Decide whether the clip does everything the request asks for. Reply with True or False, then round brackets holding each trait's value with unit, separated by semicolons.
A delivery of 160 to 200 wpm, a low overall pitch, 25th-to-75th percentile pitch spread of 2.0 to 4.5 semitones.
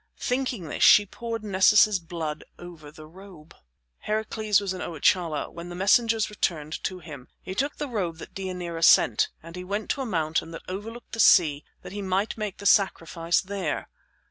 False (180 wpm; 185 Hz; 4.1 semitones)